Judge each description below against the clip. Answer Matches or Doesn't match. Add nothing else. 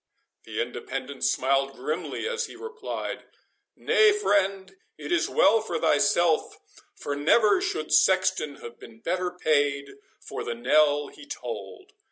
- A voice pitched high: Doesn't match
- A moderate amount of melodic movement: Doesn't match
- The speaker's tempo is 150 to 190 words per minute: Doesn't match